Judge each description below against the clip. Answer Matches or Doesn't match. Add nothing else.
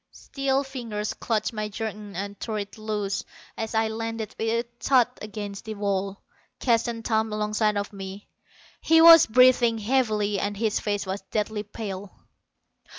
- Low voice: Doesn't match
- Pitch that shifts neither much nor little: Doesn't match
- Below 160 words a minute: Matches